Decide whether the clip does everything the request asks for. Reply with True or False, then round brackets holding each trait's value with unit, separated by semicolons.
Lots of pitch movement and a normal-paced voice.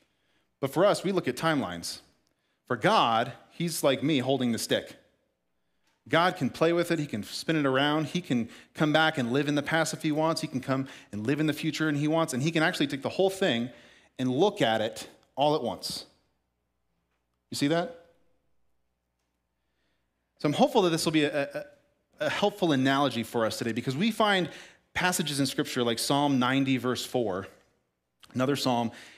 True (6.5 semitones; 195 wpm)